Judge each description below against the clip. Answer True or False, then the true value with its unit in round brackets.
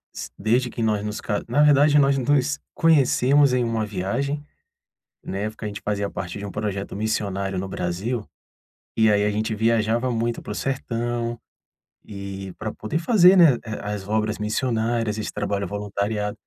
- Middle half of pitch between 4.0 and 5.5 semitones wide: False (3.5 semitones)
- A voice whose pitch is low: True (110 Hz)